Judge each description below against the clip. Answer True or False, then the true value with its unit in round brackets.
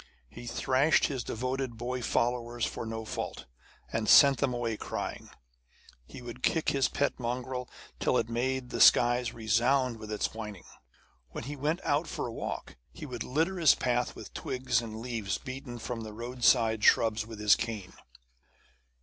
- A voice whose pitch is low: True (120 Hz)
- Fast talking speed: False (165 wpm)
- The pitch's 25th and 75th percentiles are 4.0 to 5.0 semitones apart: False (2.4 semitones)